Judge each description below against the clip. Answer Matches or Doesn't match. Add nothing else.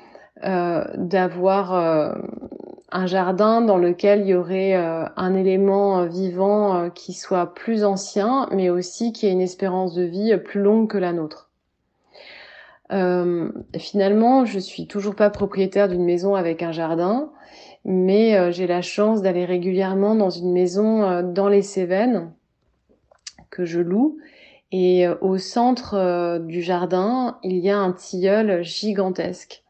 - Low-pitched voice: Doesn't match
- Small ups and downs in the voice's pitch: Matches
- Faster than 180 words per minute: Doesn't match